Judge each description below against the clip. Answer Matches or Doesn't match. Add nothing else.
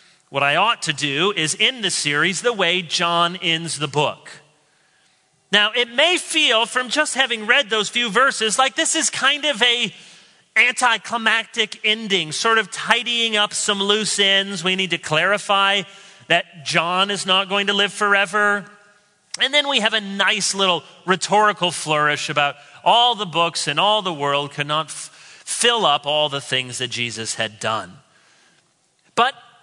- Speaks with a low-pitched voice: Doesn't match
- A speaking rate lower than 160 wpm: Doesn't match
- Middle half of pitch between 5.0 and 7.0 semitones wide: Matches